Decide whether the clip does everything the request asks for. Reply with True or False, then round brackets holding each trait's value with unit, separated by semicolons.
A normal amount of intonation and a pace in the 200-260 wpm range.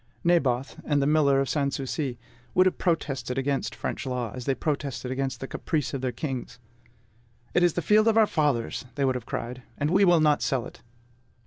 True (3.4 semitones; 205 wpm)